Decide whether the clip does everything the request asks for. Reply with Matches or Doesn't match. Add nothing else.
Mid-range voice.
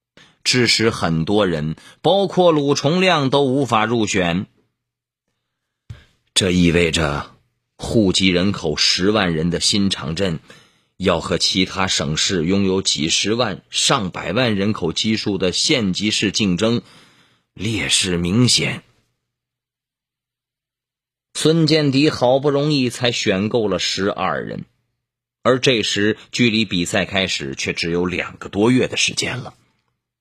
Doesn't match